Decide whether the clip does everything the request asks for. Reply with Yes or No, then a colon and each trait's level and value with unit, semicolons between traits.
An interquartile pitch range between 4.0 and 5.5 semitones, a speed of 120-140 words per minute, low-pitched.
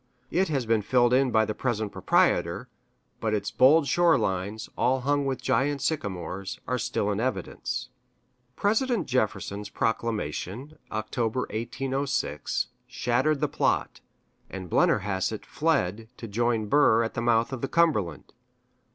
Yes: average, 4.4 semitones; slow, 135 wpm; low, 120 Hz